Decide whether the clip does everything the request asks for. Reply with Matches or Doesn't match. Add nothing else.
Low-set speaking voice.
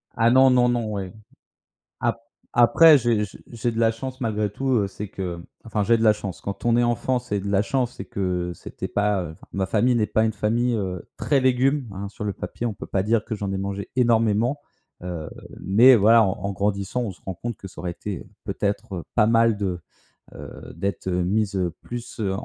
Matches